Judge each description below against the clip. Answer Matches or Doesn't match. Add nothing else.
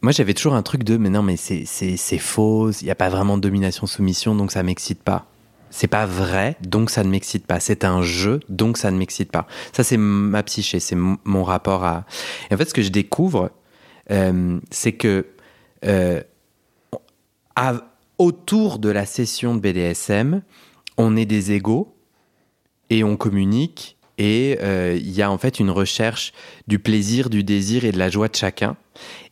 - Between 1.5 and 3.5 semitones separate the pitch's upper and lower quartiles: Matches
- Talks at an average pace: Matches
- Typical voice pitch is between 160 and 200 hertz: Doesn't match